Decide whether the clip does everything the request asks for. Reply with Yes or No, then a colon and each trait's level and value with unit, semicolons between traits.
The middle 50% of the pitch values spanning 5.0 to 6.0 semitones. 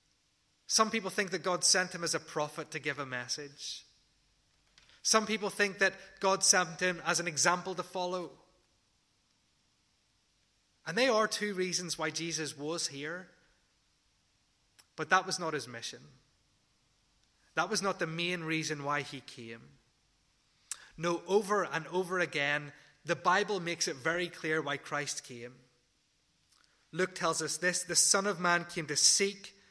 No: average, 4.3 semitones